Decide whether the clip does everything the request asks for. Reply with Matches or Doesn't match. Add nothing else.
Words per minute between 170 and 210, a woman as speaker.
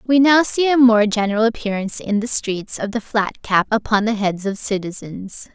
Matches